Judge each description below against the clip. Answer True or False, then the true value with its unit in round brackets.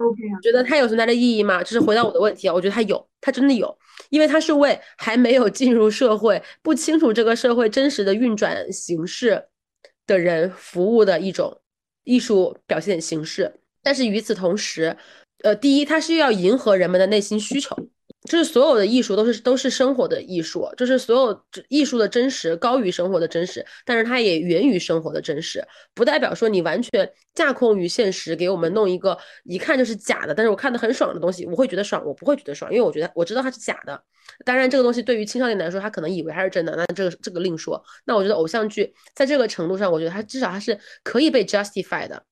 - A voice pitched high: True (220 Hz)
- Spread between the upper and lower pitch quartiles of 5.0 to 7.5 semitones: True (5.5 semitones)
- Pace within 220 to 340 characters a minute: False (355 characters per minute)